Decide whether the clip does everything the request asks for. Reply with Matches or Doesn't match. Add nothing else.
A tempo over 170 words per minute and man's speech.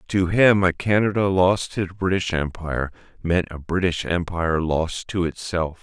Doesn't match